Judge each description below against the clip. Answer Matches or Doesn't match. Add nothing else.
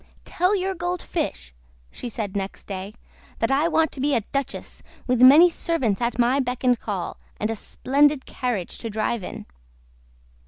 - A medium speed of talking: Matches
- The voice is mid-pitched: Doesn't match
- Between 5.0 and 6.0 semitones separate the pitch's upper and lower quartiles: Matches